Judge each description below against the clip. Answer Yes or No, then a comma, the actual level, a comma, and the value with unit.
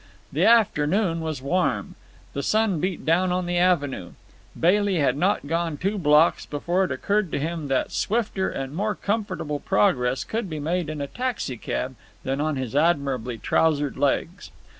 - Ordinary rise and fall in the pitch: Yes, average, 4.8 semitones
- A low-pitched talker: No, medium, 160 Hz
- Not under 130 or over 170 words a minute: Yes, average, 160 wpm